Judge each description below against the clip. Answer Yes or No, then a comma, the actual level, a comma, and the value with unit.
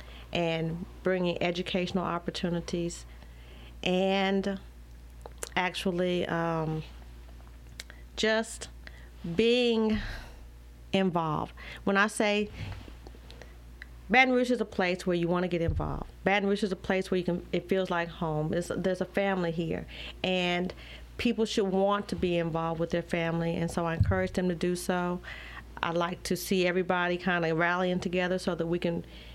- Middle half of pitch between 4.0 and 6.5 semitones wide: No, average, 3.1 semitones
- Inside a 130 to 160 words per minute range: Yes, average, 150 wpm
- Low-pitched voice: No, medium, 175 Hz